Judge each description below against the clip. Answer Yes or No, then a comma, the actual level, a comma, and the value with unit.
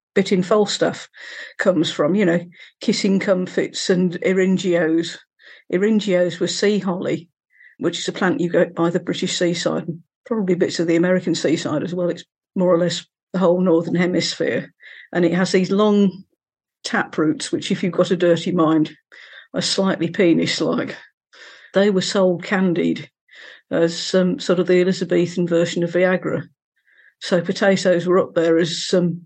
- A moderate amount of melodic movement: No, narrow, 1.8 semitones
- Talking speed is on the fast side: No, average, 170 wpm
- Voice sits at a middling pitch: Yes, medium, 180 Hz